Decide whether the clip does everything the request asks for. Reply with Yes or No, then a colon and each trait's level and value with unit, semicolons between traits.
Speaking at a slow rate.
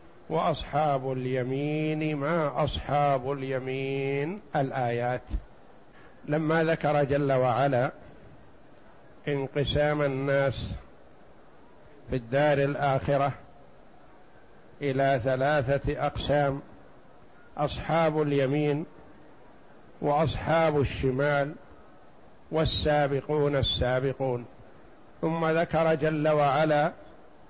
Yes: slow, 60 wpm